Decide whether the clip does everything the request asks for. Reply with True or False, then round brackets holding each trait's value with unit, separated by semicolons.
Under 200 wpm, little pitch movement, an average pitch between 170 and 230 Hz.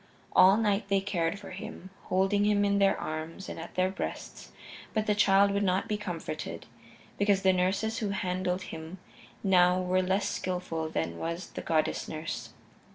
True (170 wpm; 2.0 semitones; 190 Hz)